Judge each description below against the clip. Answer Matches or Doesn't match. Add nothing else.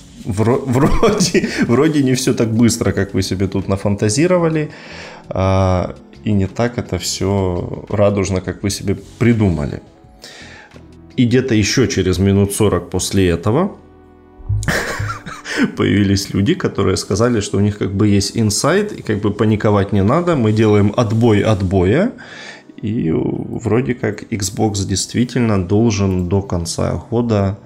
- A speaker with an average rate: Matches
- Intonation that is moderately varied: Matches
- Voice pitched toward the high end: Doesn't match